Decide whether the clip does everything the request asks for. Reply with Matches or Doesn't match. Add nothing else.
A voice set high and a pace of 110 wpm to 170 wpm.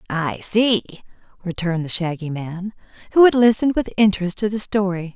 Matches